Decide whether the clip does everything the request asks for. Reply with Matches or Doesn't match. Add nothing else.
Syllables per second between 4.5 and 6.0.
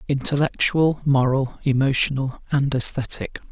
Matches